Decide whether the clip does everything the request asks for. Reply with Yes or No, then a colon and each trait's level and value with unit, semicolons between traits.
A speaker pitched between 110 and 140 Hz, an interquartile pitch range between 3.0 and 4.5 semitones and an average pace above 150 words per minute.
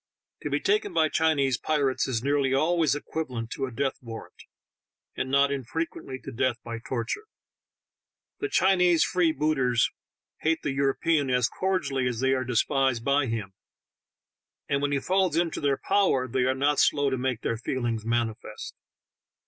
Yes: low, 135 Hz; average, 3.9 semitones; average, 160 wpm